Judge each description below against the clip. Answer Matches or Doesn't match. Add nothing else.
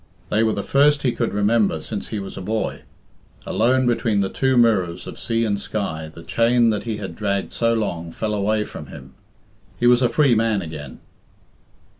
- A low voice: Matches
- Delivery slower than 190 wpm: Doesn't match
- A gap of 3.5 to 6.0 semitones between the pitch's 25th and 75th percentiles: Doesn't match